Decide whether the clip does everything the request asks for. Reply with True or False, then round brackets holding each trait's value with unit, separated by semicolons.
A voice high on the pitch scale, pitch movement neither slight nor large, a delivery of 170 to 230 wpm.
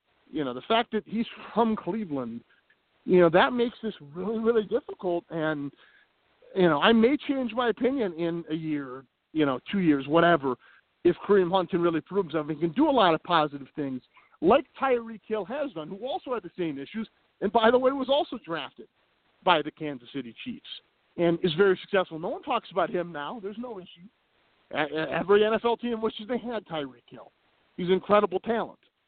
False (195 Hz; 6.0 semitones; 195 wpm)